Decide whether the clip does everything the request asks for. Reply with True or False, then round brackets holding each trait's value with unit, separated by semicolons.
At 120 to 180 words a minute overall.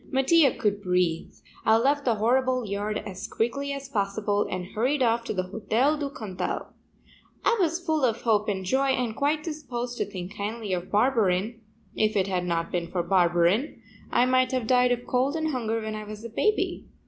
False (195 wpm)